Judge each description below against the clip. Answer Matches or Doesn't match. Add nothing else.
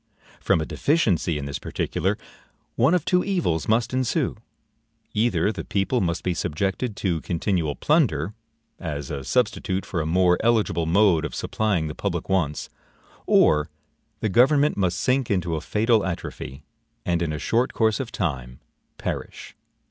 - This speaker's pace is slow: Doesn't match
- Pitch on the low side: Matches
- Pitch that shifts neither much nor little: Doesn't match